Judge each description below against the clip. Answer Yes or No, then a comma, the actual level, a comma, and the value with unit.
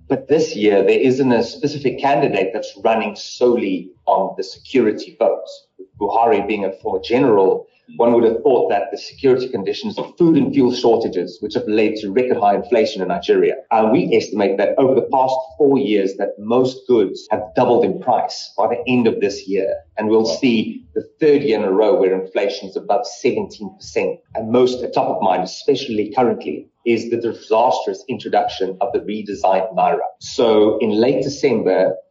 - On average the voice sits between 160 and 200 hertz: No, low, 130 Hz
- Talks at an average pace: Yes, average, 185 wpm